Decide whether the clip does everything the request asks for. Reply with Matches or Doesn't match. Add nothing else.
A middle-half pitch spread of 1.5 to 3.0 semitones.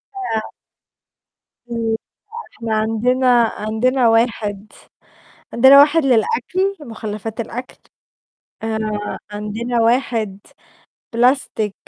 Matches